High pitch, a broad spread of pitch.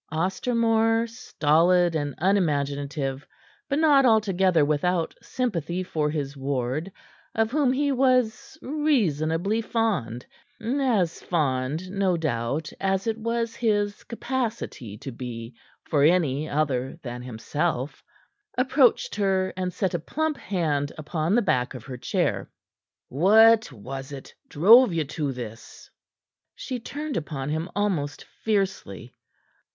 No: medium, 175 Hz; wide, 7.8 semitones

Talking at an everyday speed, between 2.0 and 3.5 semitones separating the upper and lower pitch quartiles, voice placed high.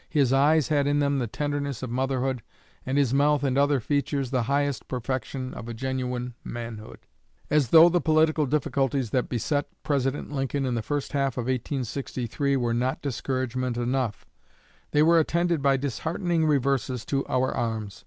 No: average, 165 wpm; narrow, 2.4 semitones; low, 135 Hz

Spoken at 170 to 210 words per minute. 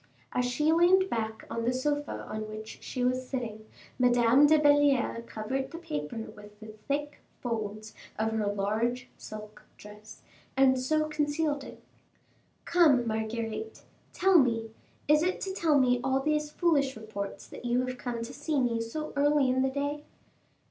No: average, 160 wpm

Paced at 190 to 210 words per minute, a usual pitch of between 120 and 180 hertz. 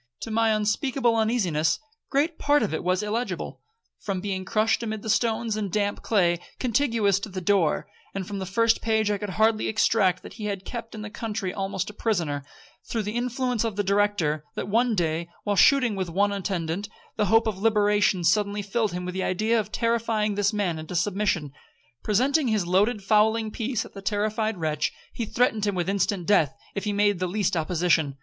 No: average, 200 wpm; high, 205 Hz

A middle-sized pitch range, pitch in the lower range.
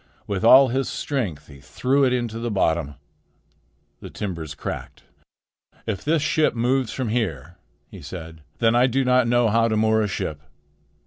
No: wide, 6.0 semitones; low, 115 Hz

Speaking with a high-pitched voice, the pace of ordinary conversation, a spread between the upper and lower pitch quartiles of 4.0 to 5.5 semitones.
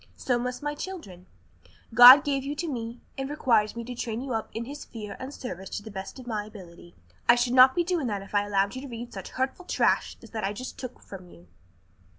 No: high, 240 Hz; fast, 240 wpm; average, 4.3 semitones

